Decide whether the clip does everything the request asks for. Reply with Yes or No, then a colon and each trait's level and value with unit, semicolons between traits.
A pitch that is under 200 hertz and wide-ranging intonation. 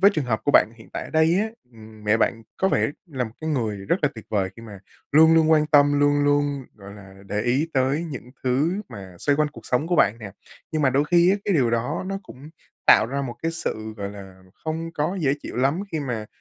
Yes: medium, 140 Hz; wide, 6.0 semitones